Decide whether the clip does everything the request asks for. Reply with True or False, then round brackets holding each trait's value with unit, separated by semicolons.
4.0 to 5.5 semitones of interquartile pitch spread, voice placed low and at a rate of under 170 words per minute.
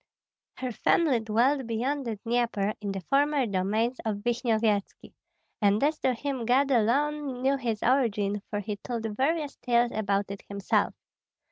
False (4.3 semitones; 235 Hz; 150 wpm)